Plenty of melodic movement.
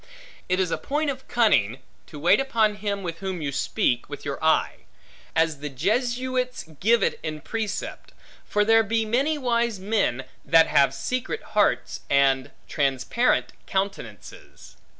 Yes: wide, 7.5 semitones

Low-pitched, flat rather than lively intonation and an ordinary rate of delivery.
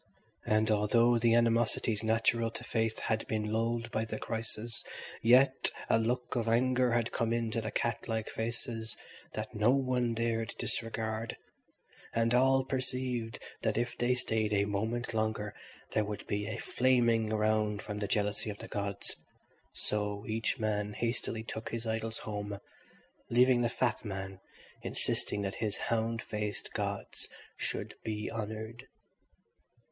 Yes: low, 115 Hz; narrow, 1.6 semitones; average, 145 wpm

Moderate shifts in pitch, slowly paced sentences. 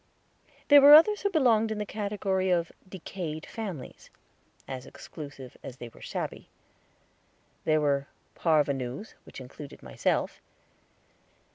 No: wide, 7.5 semitones; slow, 120 wpm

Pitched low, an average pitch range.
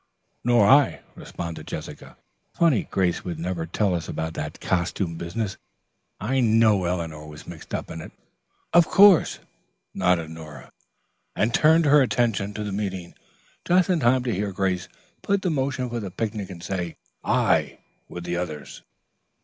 No: low, 100 Hz; wide, 5.9 semitones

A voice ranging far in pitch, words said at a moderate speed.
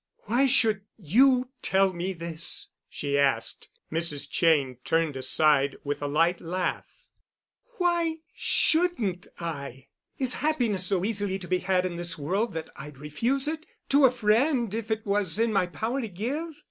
Yes: wide, 7.0 semitones; average, 155 wpm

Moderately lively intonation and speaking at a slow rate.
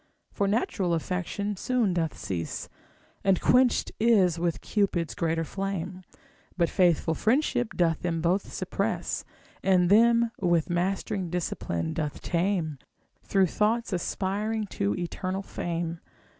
Yes: average, 3.4 semitones; slow, 120 wpm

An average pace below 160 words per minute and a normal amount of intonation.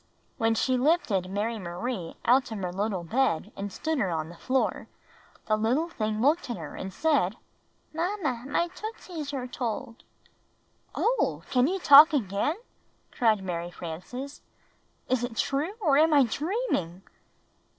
No: average, 150 wpm; wide, 7.0 semitones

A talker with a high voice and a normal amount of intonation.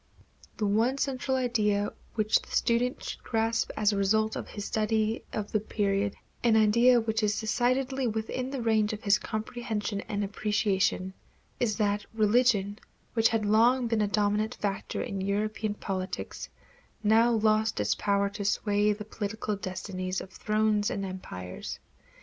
No: high, 215 Hz; narrow, 1.8 semitones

